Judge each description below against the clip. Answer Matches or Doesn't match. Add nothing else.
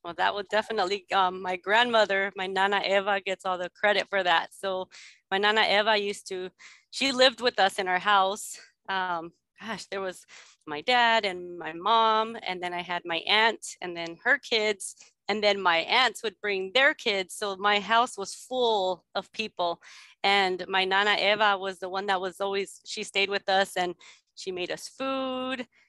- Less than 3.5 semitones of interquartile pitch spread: Matches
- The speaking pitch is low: Doesn't match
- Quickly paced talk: Doesn't match